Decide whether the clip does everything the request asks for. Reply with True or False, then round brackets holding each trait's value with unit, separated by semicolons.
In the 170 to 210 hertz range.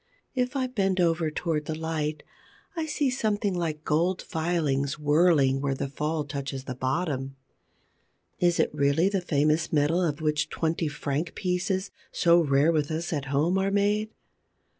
False (160 Hz)